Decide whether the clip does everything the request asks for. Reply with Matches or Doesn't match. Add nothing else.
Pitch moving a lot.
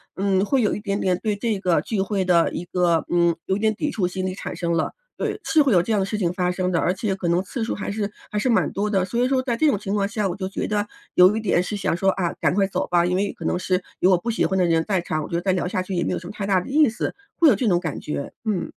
Doesn't match